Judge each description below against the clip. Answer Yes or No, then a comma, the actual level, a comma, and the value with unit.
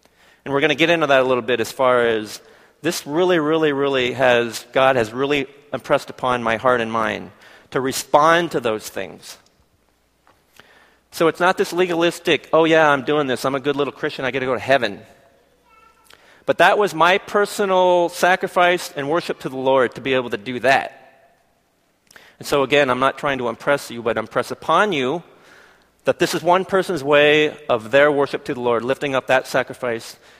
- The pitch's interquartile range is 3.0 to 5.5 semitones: Yes, average, 5.1 semitones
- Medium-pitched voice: Yes, medium, 145 Hz